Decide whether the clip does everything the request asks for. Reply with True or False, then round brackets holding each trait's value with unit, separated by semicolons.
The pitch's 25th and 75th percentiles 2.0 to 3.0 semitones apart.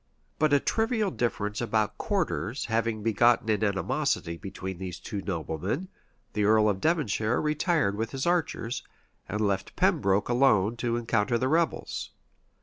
False (5.3 semitones)